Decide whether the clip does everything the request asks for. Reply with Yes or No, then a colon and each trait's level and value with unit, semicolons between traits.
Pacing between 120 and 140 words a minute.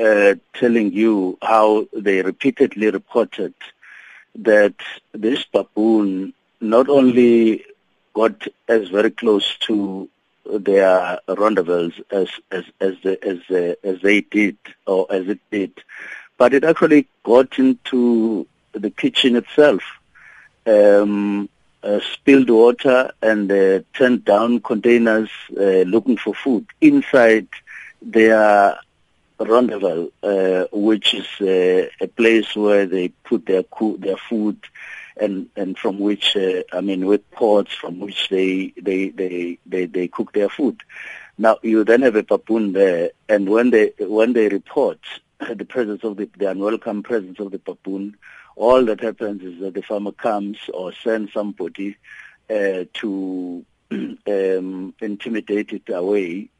Yes: slow, 135 wpm